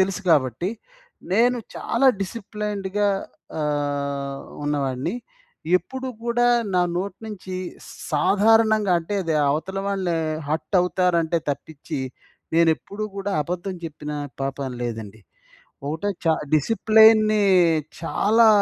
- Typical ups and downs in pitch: No, wide, 5.9 semitones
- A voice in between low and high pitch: Yes, medium, 180 Hz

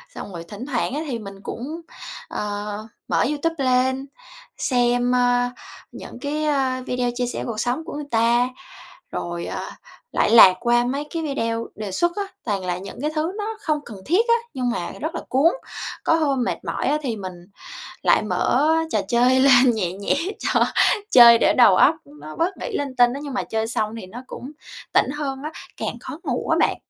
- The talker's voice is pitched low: No, high, 245 Hz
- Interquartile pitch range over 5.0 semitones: No, average, 4.5 semitones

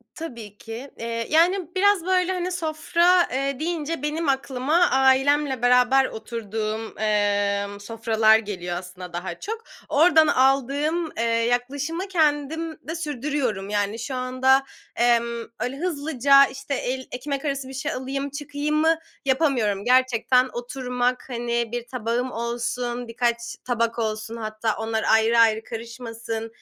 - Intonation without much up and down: No, average, 4.2 semitones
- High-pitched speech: Yes, very high, 255 Hz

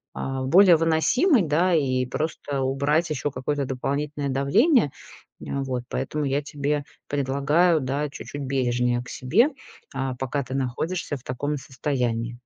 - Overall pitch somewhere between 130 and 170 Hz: Yes, medium, 140 Hz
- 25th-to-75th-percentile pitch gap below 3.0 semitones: Yes, narrow, 2.5 semitones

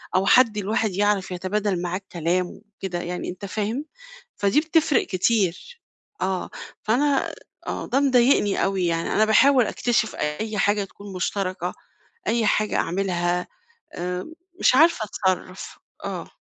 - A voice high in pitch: Yes, high, 200 Hz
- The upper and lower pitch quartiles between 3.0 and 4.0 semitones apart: Yes, average, 3.6 semitones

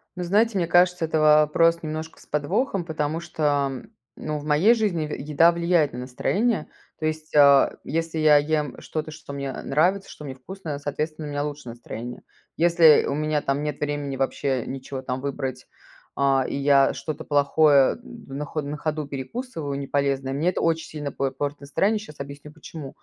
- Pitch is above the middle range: No, medium, 150 Hz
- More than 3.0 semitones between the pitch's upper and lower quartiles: No, narrow, 2.6 semitones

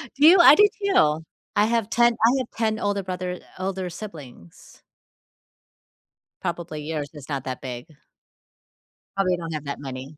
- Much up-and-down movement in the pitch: Yes, wide, 6.6 semitones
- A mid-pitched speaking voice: Yes, medium, 180 Hz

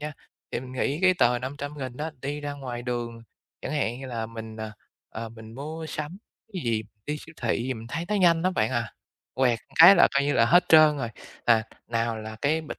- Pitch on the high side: No, low, 130 Hz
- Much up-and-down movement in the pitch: No, average, 4.7 semitones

